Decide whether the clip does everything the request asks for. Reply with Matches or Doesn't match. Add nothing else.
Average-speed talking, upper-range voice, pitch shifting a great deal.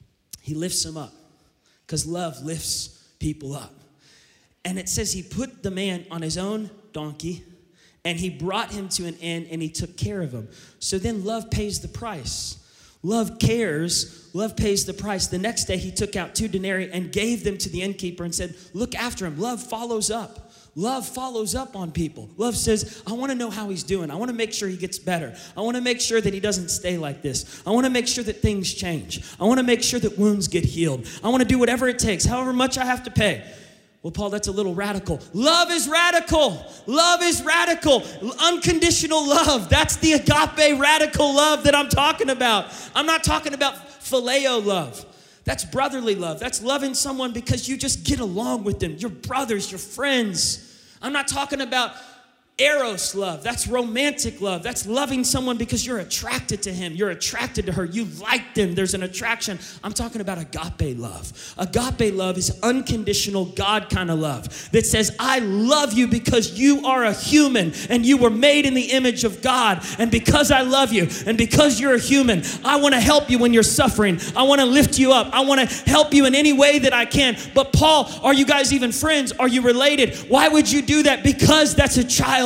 Doesn't match